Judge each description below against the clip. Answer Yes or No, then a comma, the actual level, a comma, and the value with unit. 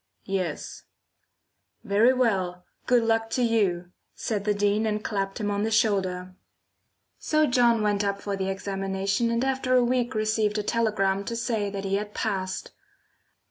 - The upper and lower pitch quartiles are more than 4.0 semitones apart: No, average, 2.9 semitones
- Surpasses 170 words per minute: No, average, 160 wpm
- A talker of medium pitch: No, high, 210 Hz